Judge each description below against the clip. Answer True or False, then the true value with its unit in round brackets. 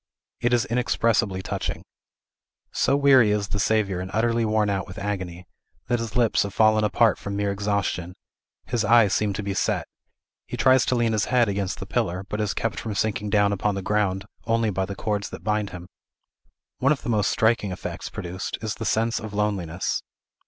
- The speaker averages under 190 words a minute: False (195 wpm)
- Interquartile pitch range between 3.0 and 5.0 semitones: False (2.6 semitones)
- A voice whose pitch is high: False (105 Hz)